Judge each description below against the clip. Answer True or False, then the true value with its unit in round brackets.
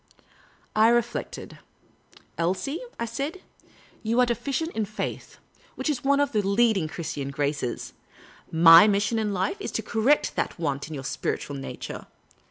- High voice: True (215 Hz)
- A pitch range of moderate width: False (6.5 semitones)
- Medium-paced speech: True (165 wpm)